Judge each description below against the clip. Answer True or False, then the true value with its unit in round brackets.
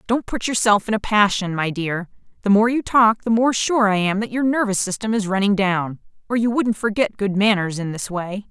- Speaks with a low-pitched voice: False (210 Hz)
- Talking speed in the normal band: False (235 wpm)